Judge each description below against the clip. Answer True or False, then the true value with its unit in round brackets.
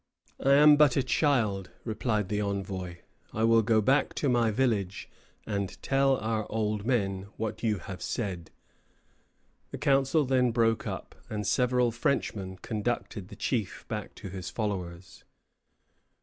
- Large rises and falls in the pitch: False (4.0 semitones)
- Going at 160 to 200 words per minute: False (145 wpm)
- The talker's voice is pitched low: True (110 Hz)